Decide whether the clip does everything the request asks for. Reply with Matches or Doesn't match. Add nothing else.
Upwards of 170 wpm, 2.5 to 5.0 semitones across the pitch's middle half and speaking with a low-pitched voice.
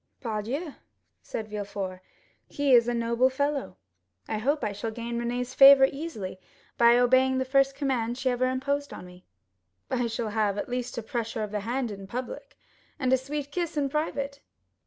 Doesn't match